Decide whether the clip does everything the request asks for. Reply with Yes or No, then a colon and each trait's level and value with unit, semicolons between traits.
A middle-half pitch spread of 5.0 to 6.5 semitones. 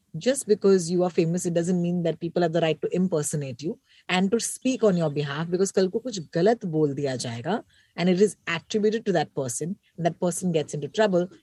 No: average, 3.6 semitones